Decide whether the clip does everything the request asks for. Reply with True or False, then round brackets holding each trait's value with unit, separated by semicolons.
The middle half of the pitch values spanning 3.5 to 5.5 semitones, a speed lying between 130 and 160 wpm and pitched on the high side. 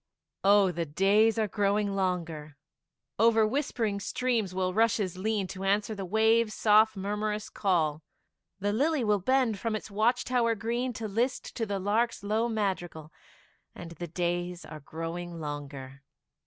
True (4.0 semitones; 150 wpm; 205 Hz)